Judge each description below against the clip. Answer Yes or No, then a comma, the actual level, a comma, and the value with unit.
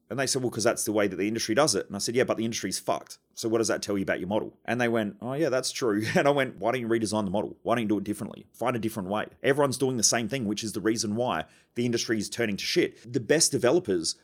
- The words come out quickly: Yes, fast, 315 wpm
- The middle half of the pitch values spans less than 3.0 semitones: Yes, narrow, 2.4 semitones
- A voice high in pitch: No, low, 115 Hz